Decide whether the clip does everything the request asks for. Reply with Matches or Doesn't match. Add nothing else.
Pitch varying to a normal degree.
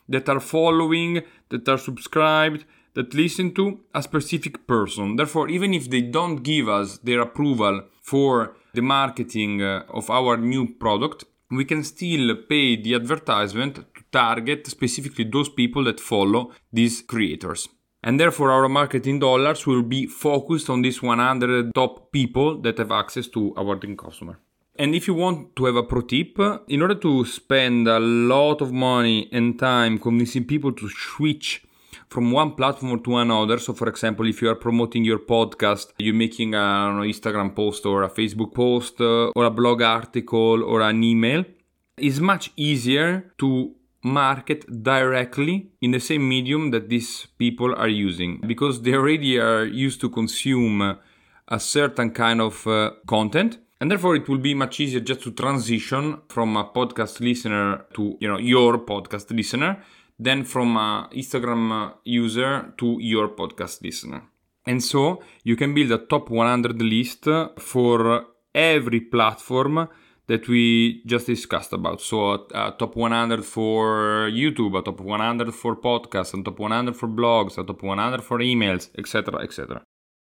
Matches